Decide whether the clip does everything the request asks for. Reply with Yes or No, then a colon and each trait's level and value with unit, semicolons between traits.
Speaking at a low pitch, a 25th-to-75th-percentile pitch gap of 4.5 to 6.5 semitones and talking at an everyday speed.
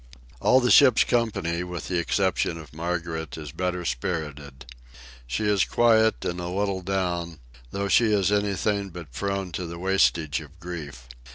No: very low, 90 Hz; average, 3.4 semitones; average, 160 wpm